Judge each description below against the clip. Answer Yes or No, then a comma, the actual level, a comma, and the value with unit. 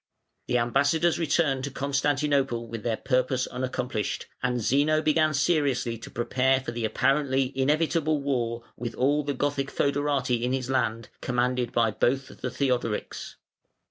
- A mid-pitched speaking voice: No, low, 130 Hz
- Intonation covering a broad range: No, average, 2.7 semitones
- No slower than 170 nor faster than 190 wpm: No, average, 140 wpm